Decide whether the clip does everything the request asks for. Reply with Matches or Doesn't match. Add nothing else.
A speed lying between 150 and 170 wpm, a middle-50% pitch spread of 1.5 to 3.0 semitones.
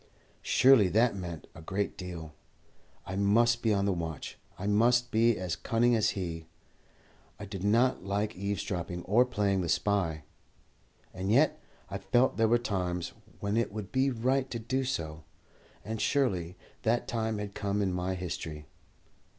Doesn't match